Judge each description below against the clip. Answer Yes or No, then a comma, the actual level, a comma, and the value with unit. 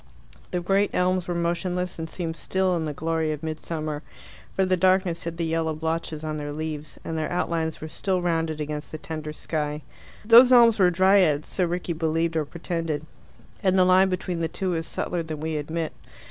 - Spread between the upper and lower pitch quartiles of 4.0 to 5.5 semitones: No, narrow, 2.6 semitones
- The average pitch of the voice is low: No, medium, 165 Hz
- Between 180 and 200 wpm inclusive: Yes, average, 195 wpm